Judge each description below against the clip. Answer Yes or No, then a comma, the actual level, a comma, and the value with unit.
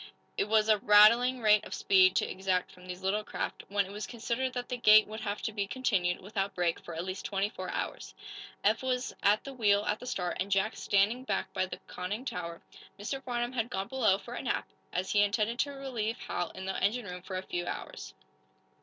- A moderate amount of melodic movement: Yes, average, 3.8 semitones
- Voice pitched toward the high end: Yes, high, 210 Hz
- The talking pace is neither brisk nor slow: No, fast, 225 wpm